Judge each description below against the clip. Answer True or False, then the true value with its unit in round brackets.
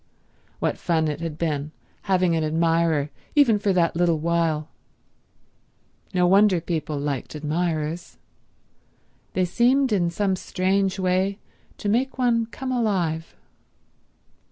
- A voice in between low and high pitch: True (175 Hz)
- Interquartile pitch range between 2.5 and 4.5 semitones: True (3.8 semitones)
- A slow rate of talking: True (120 wpm)